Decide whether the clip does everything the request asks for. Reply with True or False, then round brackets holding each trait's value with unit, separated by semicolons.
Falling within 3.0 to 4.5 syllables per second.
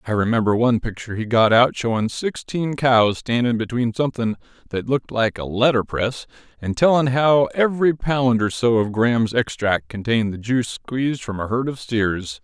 False (5.2 syllables/s)